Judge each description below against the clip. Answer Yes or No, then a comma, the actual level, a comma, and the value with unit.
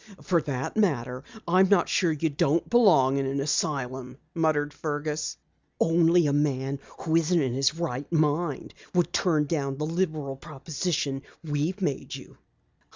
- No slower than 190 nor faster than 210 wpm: No, average, 150 wpm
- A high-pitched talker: No, medium, 150 Hz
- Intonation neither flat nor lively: Yes, average, 3.5 semitones